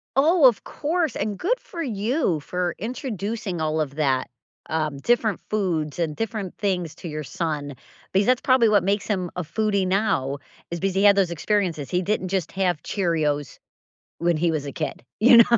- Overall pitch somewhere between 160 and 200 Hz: Yes, high, 190 Hz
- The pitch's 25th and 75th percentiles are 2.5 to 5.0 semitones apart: No, wide, 5.4 semitones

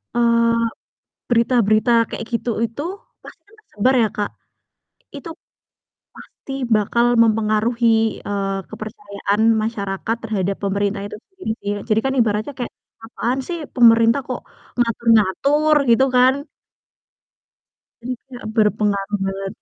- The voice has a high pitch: Yes, high, 225 Hz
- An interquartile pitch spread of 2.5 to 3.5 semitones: Yes, average, 2.8 semitones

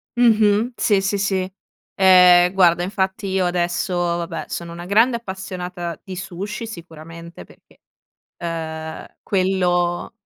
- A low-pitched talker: No, medium, 185 Hz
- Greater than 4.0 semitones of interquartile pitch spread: No, narrow, 2.2 semitones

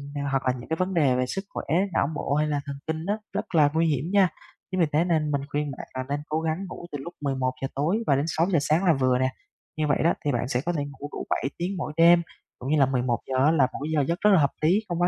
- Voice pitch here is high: No, medium, 150 Hz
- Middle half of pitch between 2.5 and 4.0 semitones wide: Yes, average, 3.7 semitones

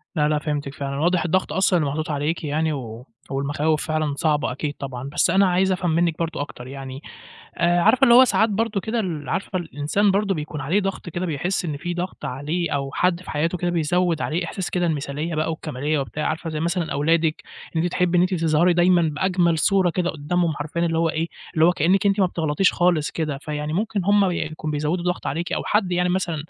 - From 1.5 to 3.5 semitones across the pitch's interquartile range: Yes, average, 3.2 semitones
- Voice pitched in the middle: Yes, medium, 165 Hz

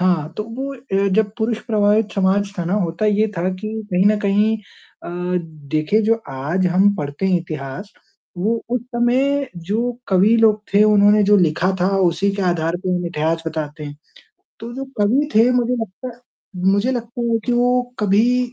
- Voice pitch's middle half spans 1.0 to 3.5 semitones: No, average, 4.3 semitones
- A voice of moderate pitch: No, high, 205 Hz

